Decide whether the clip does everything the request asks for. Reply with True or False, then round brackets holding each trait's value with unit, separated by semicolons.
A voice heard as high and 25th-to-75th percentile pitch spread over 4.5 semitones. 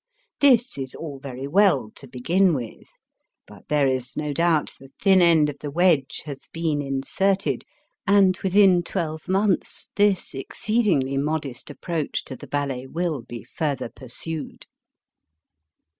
False (150 Hz; 5.3 semitones)